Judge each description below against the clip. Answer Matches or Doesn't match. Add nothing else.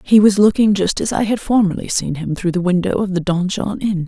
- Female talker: Matches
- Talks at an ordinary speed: Doesn't match